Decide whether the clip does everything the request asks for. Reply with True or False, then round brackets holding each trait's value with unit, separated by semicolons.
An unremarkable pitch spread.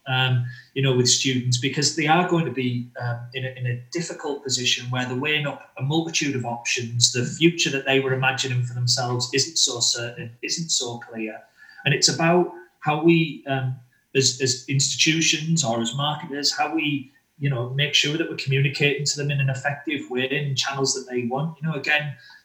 True (3.3 semitones)